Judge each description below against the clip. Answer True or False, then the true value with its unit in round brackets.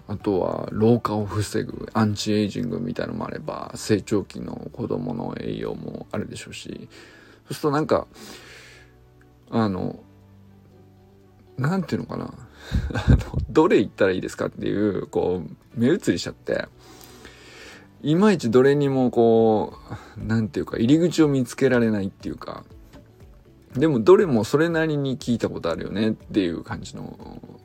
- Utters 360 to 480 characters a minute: False (315 characters per minute)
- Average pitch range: True (4.3 semitones)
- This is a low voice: True (110 Hz)